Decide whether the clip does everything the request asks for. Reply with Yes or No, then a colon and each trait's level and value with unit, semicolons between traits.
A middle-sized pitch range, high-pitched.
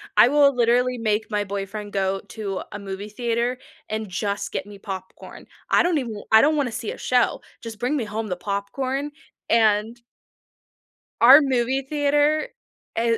Yes: average, 4.0 semitones; high, 230 Hz